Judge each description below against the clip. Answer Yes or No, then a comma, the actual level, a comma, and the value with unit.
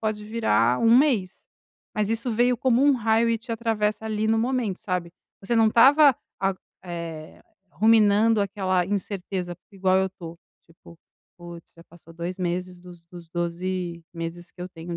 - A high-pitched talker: Yes, high, 195 Hz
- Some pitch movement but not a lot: Yes, average, 4.4 semitones